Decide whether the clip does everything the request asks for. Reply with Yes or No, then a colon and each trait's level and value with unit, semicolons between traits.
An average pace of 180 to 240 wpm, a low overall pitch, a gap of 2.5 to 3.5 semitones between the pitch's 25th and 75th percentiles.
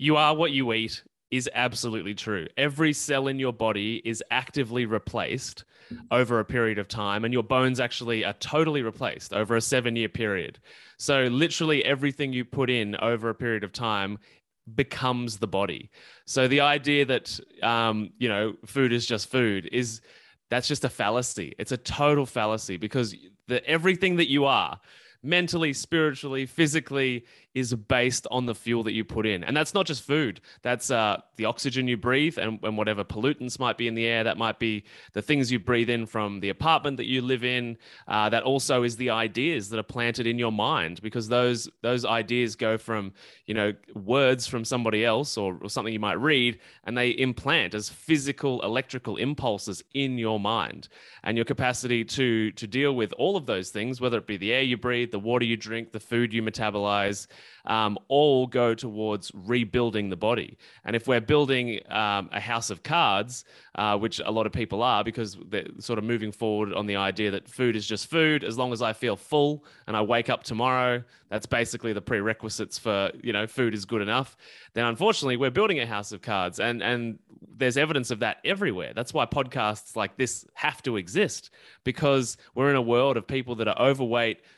Yes: average, 195 wpm; low, 120 Hz; average, 3.0 semitones